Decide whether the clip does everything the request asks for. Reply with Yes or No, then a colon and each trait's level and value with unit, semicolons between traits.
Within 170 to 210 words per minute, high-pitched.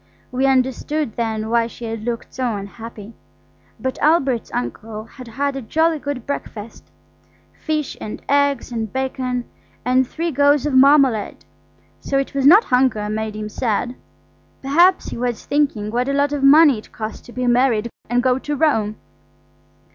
No: average, 160 wpm; very high, 255 Hz